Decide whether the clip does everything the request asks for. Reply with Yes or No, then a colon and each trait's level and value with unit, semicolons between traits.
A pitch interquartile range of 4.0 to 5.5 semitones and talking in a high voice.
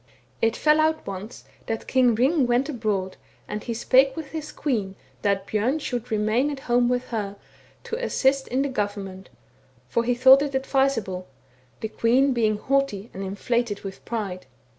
Yes: average, 4.6 semitones; high, 240 Hz